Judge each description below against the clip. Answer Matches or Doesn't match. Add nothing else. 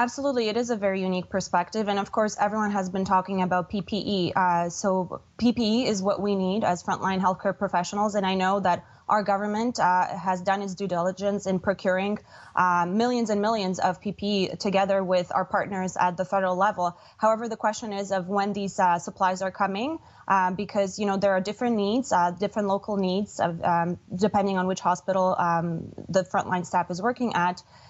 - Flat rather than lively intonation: Matches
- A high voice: Matches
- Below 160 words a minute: Doesn't match